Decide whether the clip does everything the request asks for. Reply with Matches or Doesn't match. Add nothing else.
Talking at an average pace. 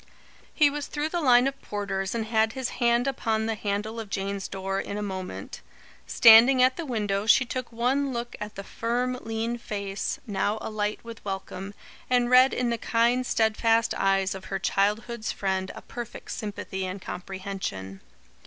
Matches